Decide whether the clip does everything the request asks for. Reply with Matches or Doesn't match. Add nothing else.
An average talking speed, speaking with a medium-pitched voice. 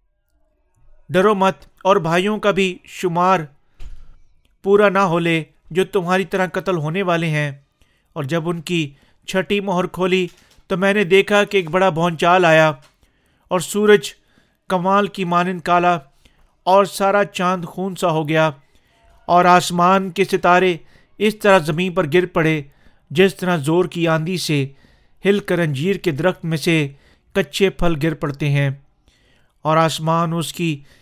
Matches